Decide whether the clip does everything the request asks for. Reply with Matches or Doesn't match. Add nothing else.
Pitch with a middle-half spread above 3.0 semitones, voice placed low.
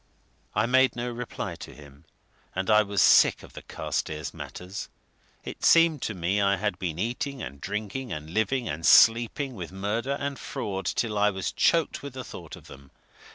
Matches